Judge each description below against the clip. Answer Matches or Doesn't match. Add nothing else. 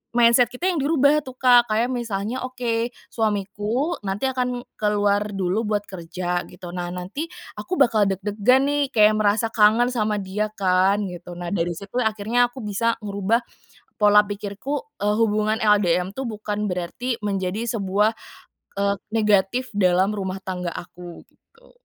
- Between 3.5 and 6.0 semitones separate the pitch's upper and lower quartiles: Matches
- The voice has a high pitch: Matches